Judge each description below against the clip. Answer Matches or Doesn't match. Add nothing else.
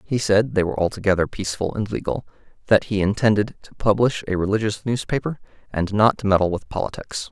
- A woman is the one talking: Doesn't match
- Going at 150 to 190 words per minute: Matches